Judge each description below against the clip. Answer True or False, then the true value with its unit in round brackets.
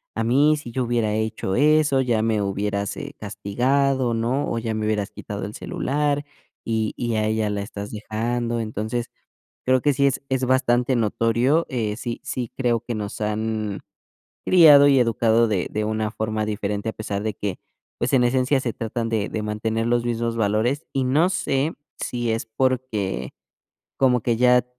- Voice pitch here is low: True (115 Hz)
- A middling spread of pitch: True (3.2 semitones)